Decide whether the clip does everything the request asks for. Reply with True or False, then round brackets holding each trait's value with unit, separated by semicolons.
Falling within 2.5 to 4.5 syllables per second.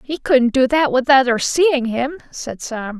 True (4.0 syllables/s)